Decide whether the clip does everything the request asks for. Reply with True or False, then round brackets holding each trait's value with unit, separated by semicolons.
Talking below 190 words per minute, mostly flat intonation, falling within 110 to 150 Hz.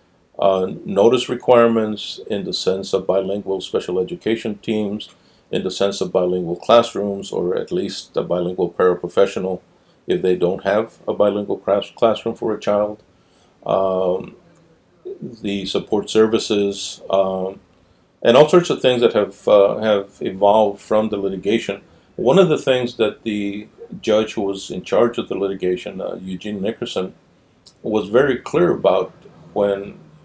False (145 wpm; 2.3 semitones; 100 Hz)